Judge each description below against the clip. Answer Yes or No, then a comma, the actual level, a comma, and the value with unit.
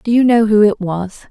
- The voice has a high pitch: Yes, high, 215 Hz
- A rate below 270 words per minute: No, fast, 275 wpm